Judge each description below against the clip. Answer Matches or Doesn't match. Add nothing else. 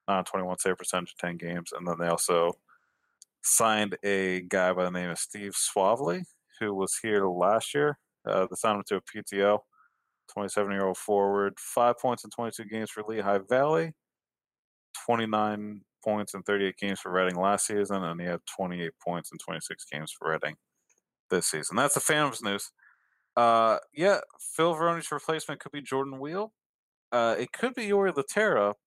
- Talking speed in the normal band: Matches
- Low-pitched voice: Matches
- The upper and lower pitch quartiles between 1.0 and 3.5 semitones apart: Doesn't match